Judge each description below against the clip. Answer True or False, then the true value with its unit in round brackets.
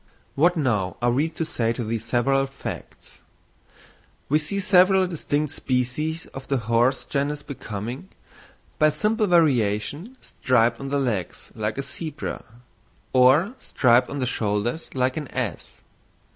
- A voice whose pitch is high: False (135 Hz)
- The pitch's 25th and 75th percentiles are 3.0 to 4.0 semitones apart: False (4.7 semitones)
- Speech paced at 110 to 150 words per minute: True (140 wpm)